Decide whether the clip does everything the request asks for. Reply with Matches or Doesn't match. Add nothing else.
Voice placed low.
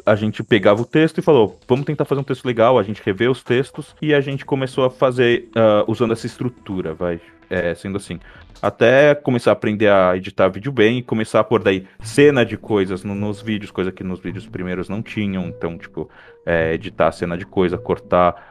Matches